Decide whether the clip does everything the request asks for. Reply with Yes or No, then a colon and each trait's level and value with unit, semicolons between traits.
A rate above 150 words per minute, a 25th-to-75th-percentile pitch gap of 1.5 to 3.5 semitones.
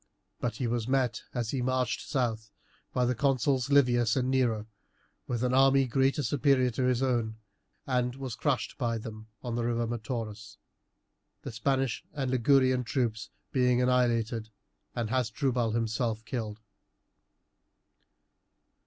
No: slow, 135 wpm; narrow, 2.4 semitones